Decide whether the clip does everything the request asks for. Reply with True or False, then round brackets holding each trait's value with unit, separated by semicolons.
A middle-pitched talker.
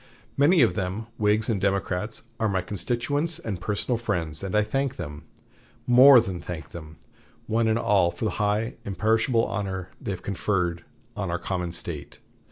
False (105 Hz)